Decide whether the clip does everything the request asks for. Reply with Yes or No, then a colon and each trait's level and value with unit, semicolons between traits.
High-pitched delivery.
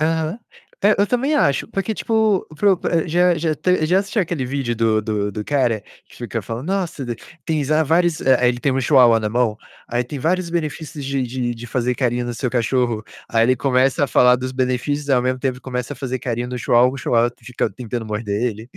No: low, 130 Hz